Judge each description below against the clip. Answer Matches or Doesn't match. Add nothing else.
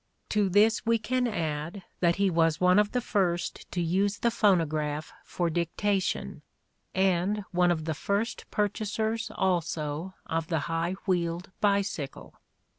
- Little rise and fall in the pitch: Doesn't match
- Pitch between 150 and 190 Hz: Matches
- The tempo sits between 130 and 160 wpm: Matches